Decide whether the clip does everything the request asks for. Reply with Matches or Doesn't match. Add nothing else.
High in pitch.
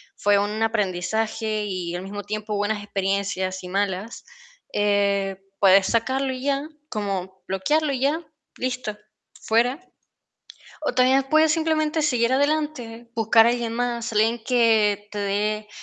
Matches